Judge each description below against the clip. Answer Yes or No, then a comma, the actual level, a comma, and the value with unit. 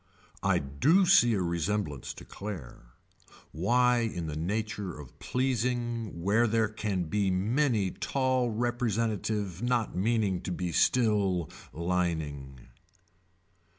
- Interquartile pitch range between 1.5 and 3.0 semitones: No, average, 5.3 semitones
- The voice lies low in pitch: Yes, low, 105 Hz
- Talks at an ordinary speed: No, slow, 115 wpm